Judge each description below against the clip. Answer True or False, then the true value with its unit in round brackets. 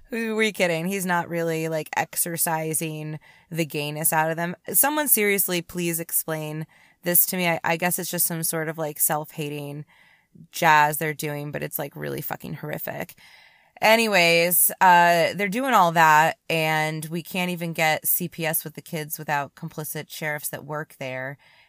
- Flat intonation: True (2.3 semitones)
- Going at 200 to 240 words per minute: False (165 wpm)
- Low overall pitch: False (165 Hz)